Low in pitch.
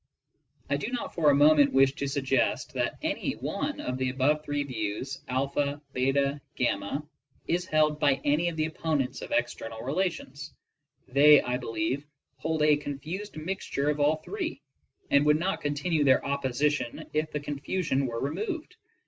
No: medium, 145 Hz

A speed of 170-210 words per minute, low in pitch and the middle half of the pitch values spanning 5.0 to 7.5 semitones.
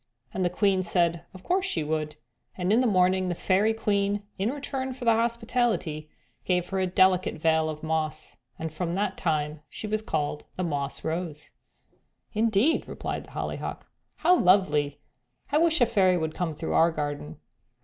No: average, 175 wpm; medium, 185 Hz; average, 5.3 semitones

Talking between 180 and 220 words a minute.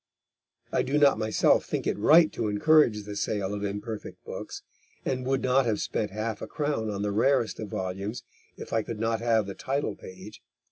Yes: average, 195 wpm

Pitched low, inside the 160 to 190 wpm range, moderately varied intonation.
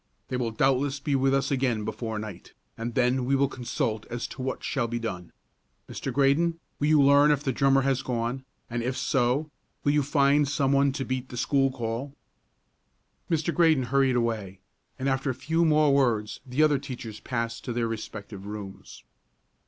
Yes: low, 130 Hz; average, 185 wpm; average, 3.0 semitones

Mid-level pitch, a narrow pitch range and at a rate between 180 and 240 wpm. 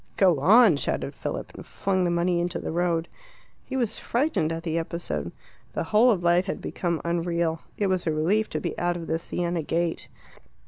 Yes: medium, 175 Hz; narrow, 2.2 semitones; average, 195 wpm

